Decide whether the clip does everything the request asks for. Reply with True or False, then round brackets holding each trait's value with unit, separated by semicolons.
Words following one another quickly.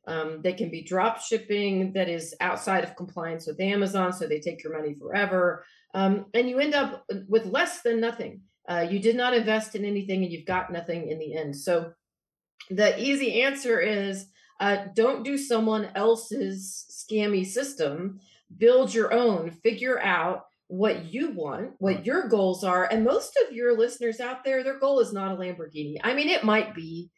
False (185 wpm)